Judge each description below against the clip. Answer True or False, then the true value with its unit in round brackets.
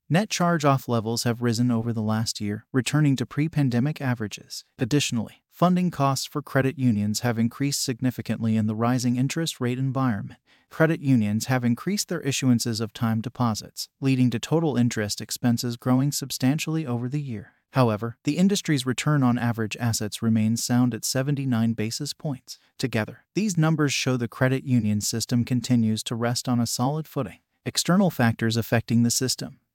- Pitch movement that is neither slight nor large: True (3.3 semitones)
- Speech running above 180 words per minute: False (165 wpm)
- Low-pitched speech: True (125 Hz)